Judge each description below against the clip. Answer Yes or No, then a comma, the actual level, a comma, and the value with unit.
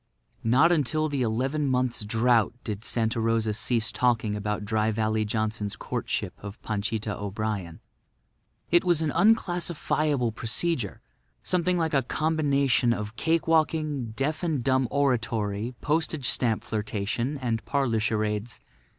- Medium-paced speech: No, slow, 130 wpm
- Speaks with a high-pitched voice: No, low, 120 Hz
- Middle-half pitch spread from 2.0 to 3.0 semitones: No, wide, 5.4 semitones